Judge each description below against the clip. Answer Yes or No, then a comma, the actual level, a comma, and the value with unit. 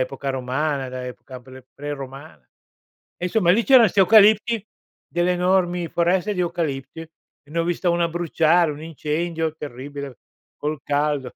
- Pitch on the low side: No, medium, 160 Hz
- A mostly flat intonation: No, average, 4.2 semitones